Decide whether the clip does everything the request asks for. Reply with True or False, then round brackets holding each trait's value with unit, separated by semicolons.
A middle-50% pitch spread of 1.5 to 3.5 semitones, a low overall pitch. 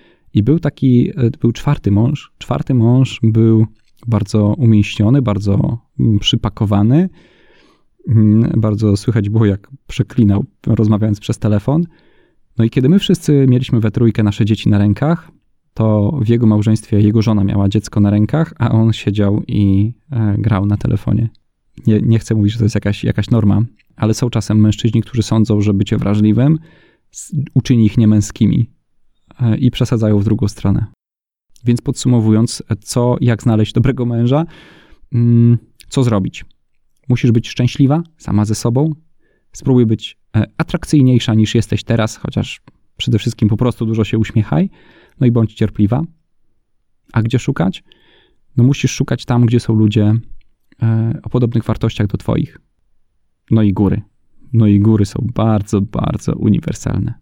True (2.9 semitones; 110 Hz)